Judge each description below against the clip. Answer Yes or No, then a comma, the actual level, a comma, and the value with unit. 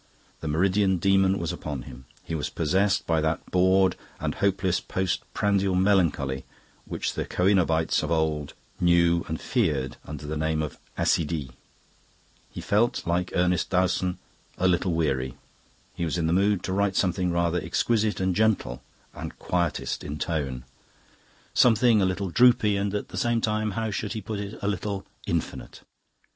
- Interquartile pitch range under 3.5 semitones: No, average, 3.8 semitones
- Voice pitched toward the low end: Yes, very low, 90 Hz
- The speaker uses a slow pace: No, average, 160 wpm